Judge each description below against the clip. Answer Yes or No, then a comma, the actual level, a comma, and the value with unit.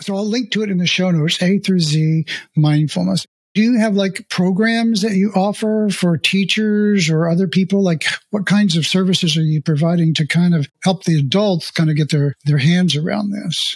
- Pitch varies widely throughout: No, average, 4.0 semitones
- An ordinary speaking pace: No, fast, 210 wpm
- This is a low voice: No, medium, 185 Hz